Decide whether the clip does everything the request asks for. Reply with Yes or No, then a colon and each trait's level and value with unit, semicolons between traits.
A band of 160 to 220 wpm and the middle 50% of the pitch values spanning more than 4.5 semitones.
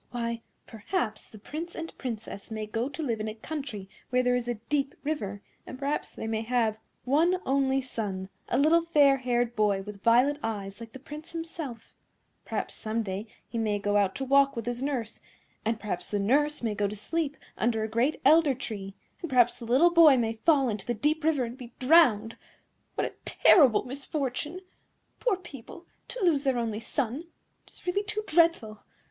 Yes: average, 195 wpm; average, 5.2 semitones